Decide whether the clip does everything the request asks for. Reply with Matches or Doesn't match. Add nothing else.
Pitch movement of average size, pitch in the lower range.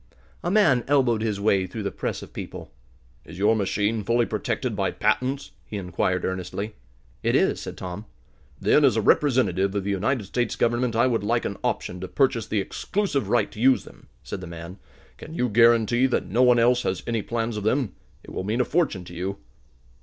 Matches